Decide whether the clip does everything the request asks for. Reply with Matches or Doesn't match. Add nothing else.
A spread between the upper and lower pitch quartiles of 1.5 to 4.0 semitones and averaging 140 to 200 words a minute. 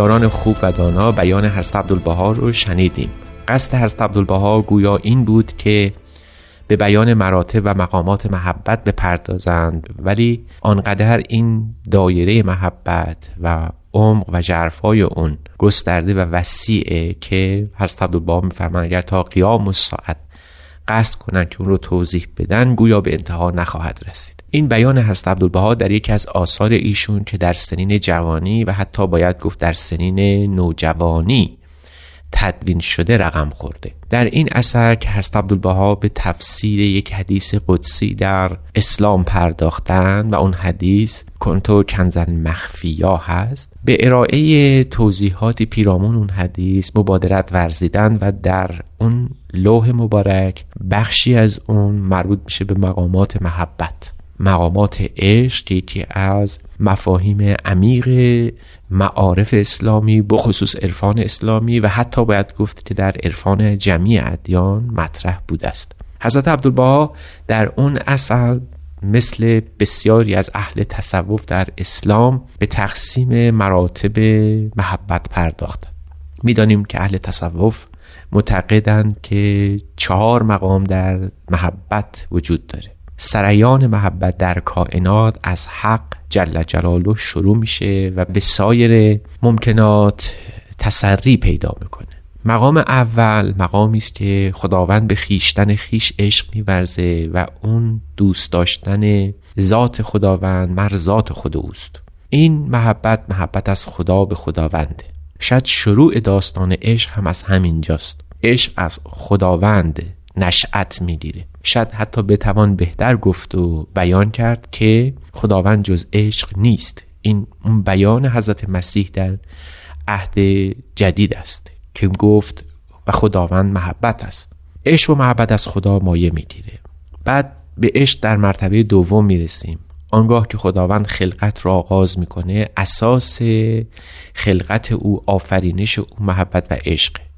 Doesn't match